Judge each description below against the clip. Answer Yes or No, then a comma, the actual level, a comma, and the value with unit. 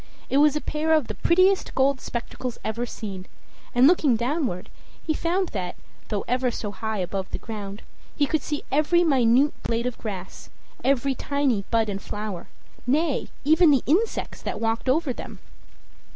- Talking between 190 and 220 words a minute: No, average, 165 wpm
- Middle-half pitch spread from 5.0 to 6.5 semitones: Yes, wide, 5.5 semitones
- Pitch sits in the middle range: No, very high, 255 Hz